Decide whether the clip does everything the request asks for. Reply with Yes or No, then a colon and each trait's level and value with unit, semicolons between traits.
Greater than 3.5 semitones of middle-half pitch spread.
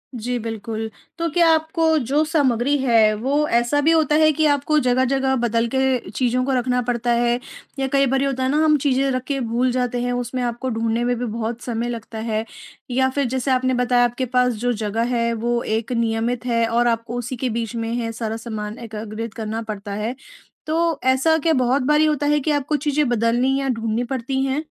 No: average, 2.8 semitones